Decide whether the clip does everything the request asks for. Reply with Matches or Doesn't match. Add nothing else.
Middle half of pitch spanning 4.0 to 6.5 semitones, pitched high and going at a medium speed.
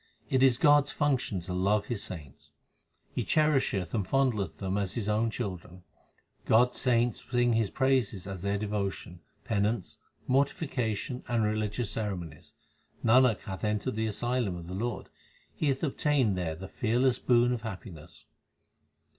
Doesn't match